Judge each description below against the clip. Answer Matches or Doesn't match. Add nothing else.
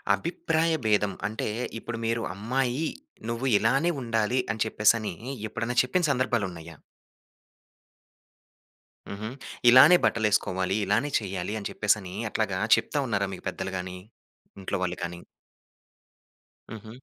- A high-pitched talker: Doesn't match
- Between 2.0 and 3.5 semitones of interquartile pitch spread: Doesn't match